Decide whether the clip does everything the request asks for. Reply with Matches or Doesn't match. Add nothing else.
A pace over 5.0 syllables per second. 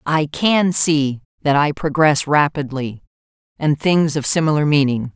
Doesn't match